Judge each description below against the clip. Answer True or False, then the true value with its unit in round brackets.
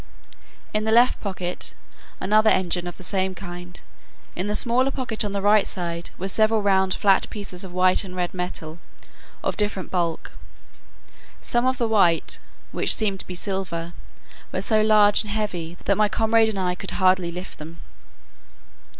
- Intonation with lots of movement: False (3.1 semitones)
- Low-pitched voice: False (190 Hz)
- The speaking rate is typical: True (170 wpm)